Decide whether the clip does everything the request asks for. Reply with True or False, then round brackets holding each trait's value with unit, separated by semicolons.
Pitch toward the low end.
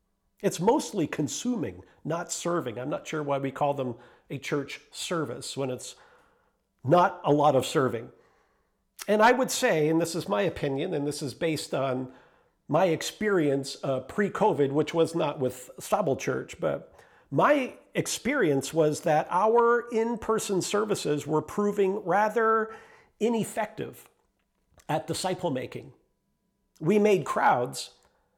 False (165 Hz)